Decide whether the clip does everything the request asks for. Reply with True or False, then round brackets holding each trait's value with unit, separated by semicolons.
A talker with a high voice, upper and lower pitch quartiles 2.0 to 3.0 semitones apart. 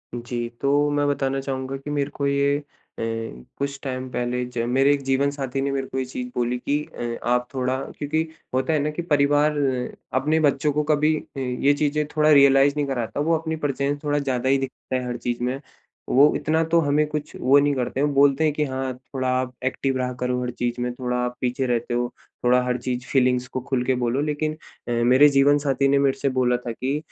False (135 Hz; 2.5 semitones)